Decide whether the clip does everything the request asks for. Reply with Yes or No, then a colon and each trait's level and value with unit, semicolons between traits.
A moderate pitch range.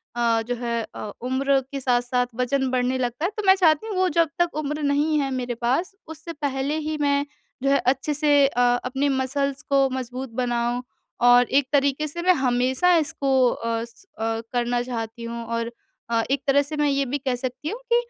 Yes: average, 3.0 semitones